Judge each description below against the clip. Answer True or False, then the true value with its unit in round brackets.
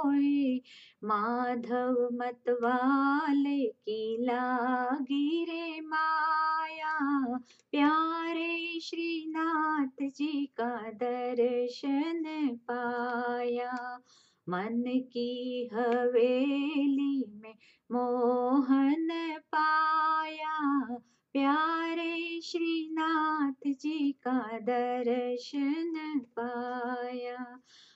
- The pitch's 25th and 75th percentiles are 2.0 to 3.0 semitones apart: False (4.2 semitones)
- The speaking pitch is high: True (270 Hz)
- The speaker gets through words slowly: True (50 wpm)